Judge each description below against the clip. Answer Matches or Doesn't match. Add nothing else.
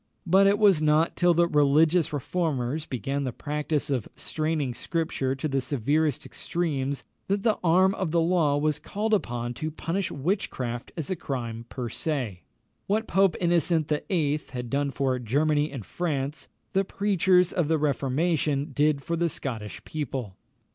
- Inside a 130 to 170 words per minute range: Matches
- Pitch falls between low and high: Matches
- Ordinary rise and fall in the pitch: Matches